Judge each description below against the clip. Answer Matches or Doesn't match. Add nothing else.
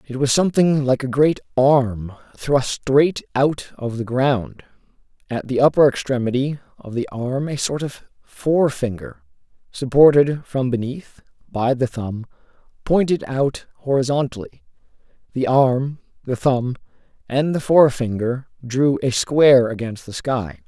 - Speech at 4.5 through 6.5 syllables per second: Doesn't match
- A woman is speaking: Doesn't match